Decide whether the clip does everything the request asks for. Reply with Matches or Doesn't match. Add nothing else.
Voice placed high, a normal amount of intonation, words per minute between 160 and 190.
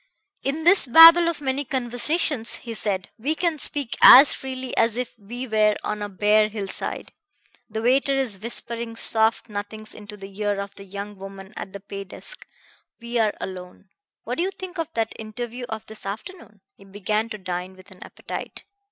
Matches